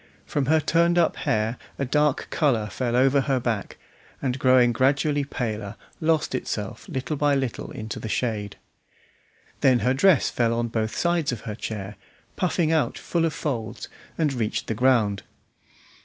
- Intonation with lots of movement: No, average, 4.7 semitones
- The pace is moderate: Yes, average, 160 wpm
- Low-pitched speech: Yes, low, 130 Hz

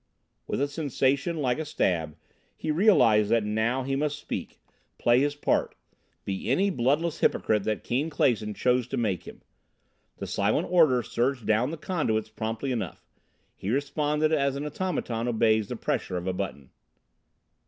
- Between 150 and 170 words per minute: Yes, average, 160 wpm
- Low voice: Yes, low, 125 Hz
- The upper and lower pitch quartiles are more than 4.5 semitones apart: Yes, average, 5.2 semitones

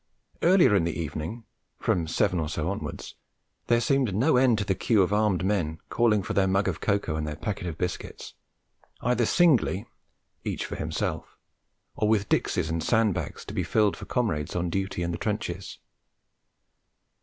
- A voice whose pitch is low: Yes, low, 100 Hz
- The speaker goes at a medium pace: Yes, average, 180 wpm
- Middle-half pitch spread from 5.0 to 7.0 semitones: No, average, 4.6 semitones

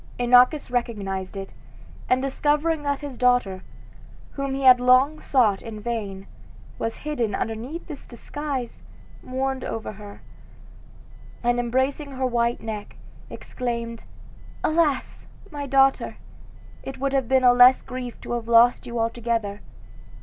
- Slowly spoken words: Yes, slow, 130 wpm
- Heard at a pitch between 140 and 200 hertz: No, high, 245 Hz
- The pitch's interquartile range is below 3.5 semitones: Yes, average, 2.8 semitones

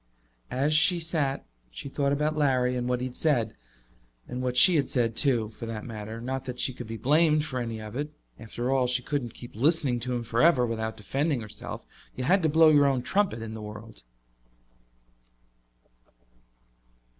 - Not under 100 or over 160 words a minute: No, average, 185 wpm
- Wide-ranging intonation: No, average, 4.1 semitones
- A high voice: No, low, 125 Hz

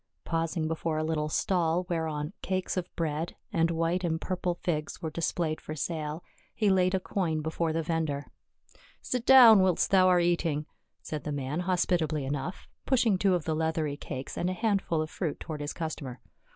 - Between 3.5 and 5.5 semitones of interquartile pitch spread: No, average, 2.7 semitones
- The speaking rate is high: No, average, 180 wpm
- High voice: No, medium, 165 Hz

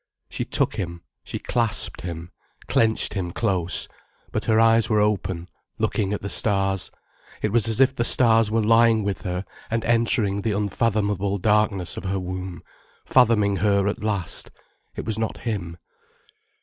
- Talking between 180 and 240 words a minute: No, average, 160 wpm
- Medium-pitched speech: No, low, 105 Hz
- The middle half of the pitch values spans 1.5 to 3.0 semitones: Yes, average, 2.7 semitones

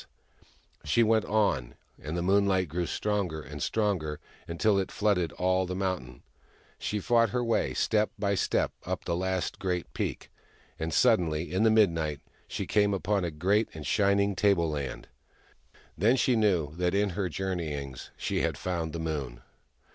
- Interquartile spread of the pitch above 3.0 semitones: Yes, average, 4.3 semitones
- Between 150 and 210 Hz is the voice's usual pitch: No, very low, 95 Hz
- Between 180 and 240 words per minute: No, average, 165 wpm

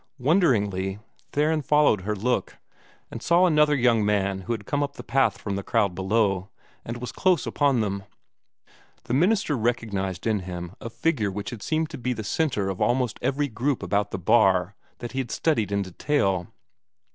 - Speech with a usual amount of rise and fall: No, wide, 6.3 semitones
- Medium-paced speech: Yes, average, 180 wpm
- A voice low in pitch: Yes, low, 115 Hz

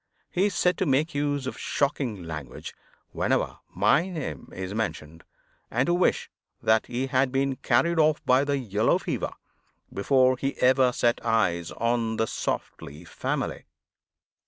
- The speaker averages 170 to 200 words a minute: No, average, 150 wpm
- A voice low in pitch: Yes, low, 130 Hz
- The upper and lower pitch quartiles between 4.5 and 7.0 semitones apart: Yes, average, 4.8 semitones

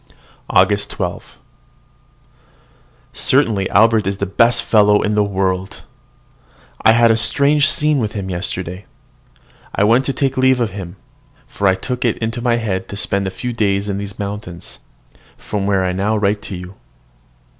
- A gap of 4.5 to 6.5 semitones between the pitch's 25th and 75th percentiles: No, average, 3.2 semitones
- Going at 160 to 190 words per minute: Yes, average, 165 wpm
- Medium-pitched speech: No, low, 105 Hz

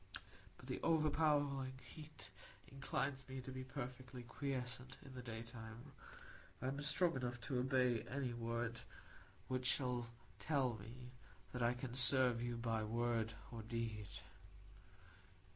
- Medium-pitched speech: No, low, 125 Hz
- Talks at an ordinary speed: No, slow, 130 wpm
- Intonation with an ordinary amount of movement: No, narrow, 2.3 semitones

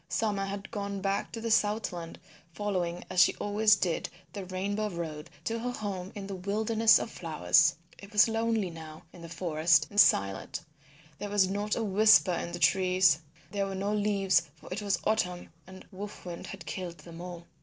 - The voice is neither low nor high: No, high, 195 Hz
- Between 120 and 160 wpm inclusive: No, average, 185 wpm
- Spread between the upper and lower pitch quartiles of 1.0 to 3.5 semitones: Yes, average, 2.9 semitones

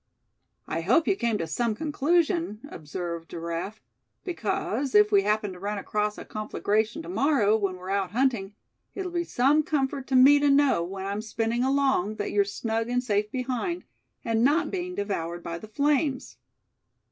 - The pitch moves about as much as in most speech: No, wide, 5.7 semitones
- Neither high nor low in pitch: No, high, 225 Hz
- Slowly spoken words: No, average, 170 wpm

